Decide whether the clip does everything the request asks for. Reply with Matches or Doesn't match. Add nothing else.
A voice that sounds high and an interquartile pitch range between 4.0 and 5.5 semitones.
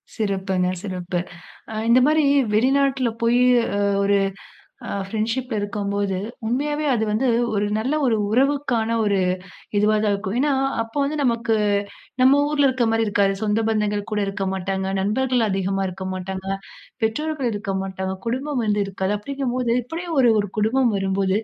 Matches